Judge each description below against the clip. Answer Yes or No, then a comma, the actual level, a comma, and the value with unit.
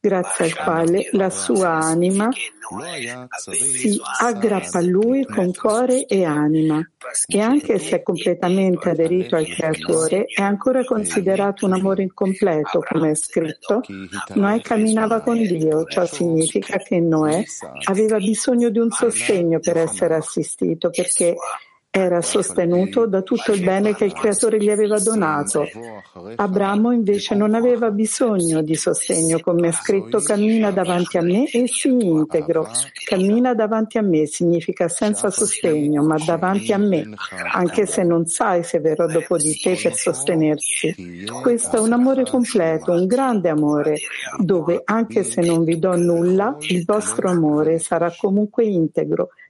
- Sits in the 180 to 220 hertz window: Yes, medium, 185 Hz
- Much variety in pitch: No, average, 4.7 semitones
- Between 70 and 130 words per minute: No, average, 145 wpm